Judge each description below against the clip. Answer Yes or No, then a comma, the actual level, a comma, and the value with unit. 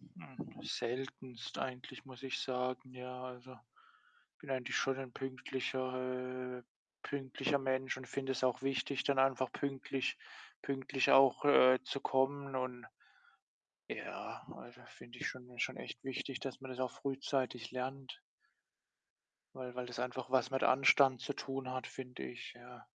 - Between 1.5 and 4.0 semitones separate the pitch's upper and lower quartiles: No, narrow, 1.0 semitones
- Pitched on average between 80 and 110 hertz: No, low, 130 Hz